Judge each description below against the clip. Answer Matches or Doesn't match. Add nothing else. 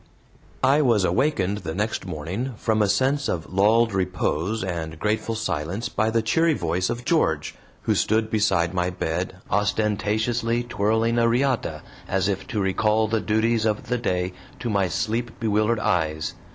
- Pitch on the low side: Matches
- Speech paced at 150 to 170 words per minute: Matches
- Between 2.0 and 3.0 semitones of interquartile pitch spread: Doesn't match